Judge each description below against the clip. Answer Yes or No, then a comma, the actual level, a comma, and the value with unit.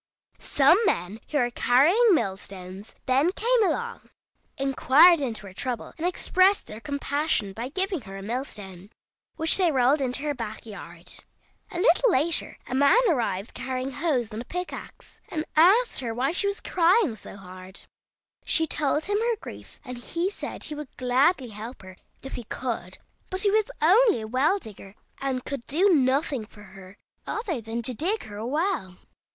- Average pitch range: No, wide, 7.8 semitones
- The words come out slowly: No, average, 175 wpm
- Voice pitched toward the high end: Yes, very high, 270 Hz